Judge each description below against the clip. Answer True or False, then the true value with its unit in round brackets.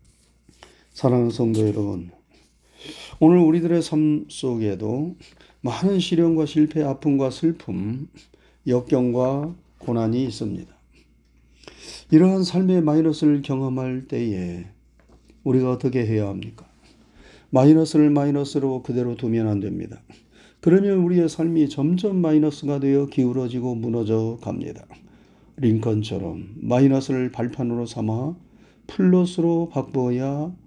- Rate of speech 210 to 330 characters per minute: True (265 characters per minute)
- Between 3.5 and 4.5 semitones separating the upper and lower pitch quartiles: False (5.3 semitones)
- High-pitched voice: False (130 Hz)